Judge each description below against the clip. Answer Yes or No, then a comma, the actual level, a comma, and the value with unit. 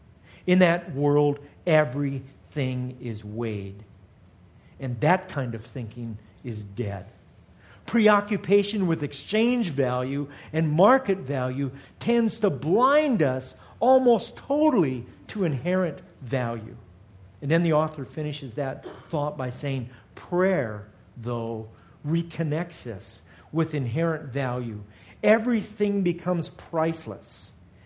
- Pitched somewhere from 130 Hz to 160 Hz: Yes, medium, 140 Hz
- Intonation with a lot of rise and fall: Yes, wide, 7.2 semitones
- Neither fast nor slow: No, slow, 105 wpm